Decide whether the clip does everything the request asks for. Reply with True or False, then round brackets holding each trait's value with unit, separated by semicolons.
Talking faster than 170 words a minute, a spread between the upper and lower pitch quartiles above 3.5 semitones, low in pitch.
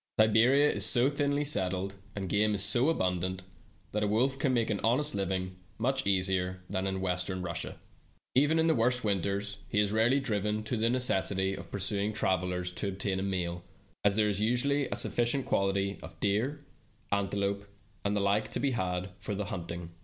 True (190 wpm; 4.0 semitones; 100 Hz)